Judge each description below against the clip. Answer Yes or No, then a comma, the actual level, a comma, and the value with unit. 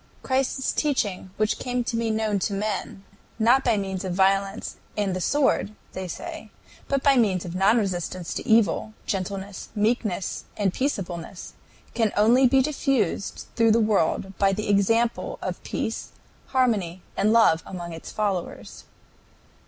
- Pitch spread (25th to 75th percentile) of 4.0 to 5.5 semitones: No, average, 3.4 semitones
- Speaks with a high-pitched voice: Yes, high, 210 Hz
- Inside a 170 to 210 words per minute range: No, average, 150 wpm